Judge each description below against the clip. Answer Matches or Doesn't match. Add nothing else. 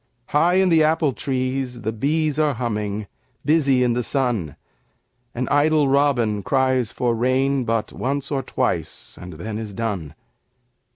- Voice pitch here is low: Matches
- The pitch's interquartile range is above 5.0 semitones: Doesn't match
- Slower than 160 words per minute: Matches